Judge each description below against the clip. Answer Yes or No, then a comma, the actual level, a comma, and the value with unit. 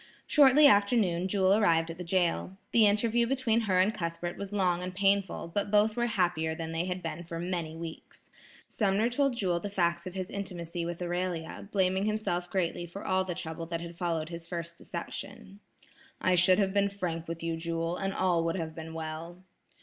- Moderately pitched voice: Yes, medium, 180 Hz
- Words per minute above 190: Yes, average, 200 wpm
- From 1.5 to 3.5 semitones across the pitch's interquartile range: Yes, average, 3.0 semitones